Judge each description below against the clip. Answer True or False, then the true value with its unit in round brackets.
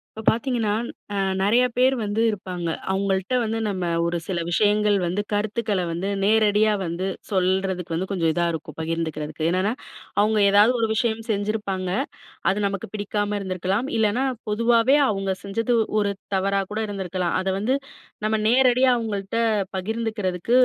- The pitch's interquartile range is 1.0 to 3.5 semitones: True (2.9 semitones)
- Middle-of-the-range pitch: False (205 Hz)